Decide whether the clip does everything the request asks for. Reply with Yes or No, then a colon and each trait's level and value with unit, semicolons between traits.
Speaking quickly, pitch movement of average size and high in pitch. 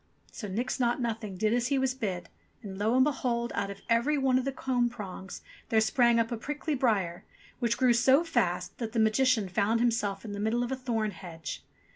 Yes: fast, 215 wpm; average, 3.8 semitones; high, 235 Hz